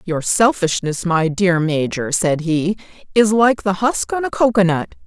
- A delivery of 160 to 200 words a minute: Yes, average, 165 wpm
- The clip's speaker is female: Yes, female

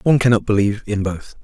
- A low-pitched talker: Yes, low, 105 Hz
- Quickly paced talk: Yes, fast, 210 wpm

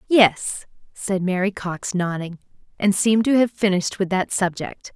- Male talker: No, female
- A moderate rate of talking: Yes, average, 160 wpm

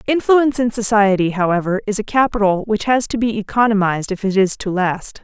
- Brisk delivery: No, average, 195 wpm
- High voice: Yes, high, 210 Hz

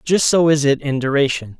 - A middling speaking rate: No, fast, 225 wpm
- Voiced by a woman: No, male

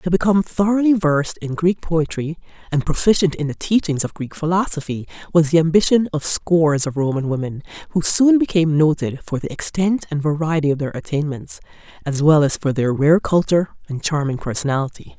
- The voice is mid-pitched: Yes, medium, 160 Hz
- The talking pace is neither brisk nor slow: Yes, average, 180 wpm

